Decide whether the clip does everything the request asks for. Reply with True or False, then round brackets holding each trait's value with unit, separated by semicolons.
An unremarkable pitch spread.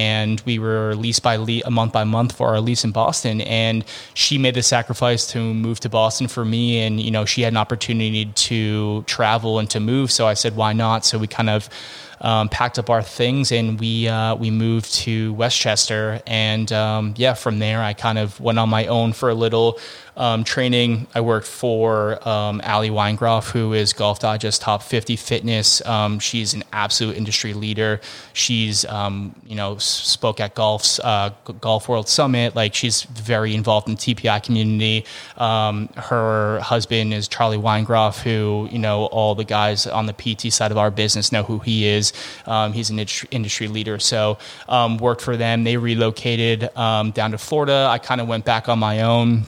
False (1.5 semitones)